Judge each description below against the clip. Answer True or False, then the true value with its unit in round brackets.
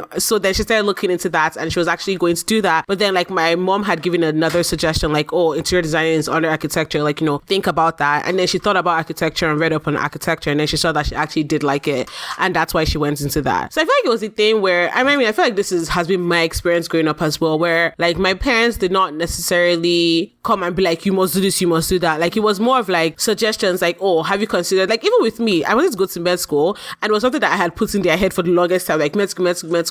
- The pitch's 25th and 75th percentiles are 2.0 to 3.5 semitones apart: True (3.1 semitones)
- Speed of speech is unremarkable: False (305 wpm)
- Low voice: False (175 Hz)